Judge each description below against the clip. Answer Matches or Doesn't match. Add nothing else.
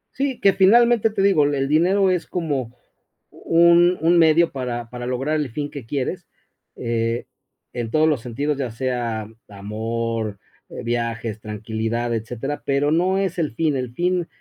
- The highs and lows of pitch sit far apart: Matches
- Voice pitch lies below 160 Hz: Matches